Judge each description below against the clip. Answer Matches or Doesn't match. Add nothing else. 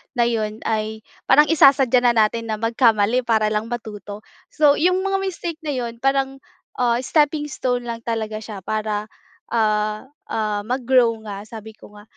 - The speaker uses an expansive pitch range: Doesn't match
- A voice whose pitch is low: Doesn't match